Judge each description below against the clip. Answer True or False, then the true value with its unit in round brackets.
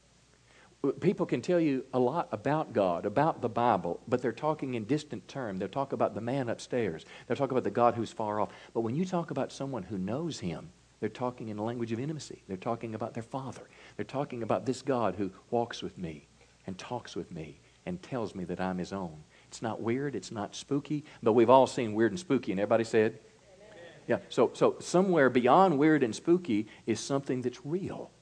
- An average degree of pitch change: True (4.3 semitones)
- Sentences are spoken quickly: True (215 wpm)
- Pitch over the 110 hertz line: True (120 Hz)